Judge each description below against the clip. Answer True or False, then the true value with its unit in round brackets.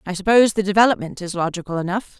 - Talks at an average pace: True (190 wpm)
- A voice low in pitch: False (195 Hz)